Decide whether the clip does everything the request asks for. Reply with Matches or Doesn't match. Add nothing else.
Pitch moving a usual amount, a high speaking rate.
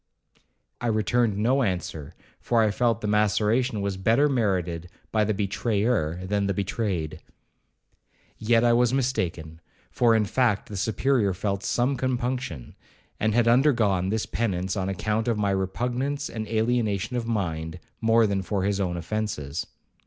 Doesn't match